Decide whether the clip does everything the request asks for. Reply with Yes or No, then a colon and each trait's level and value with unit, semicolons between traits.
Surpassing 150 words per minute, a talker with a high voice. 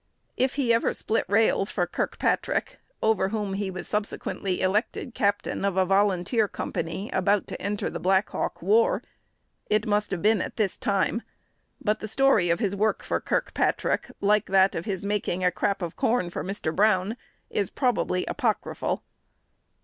Yes: average, 165 wpm; high, 205 Hz